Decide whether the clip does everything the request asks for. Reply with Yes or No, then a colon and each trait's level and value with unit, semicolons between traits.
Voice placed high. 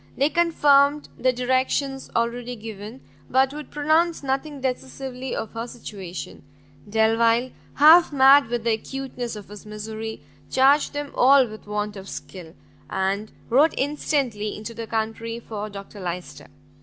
Yes: high, 240 Hz